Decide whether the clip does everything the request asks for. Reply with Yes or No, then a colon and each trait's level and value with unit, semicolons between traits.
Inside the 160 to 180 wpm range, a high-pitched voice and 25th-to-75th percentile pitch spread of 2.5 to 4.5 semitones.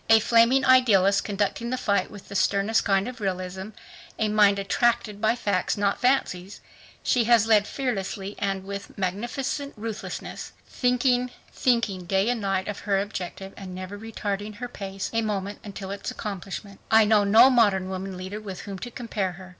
Yes: average, 170 wpm; high, 205 Hz; average, 2.8 semitones